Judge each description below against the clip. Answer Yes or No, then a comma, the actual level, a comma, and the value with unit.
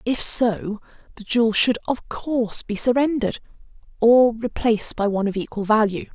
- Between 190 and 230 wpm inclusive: No, average, 145 wpm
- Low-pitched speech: No, high, 230 Hz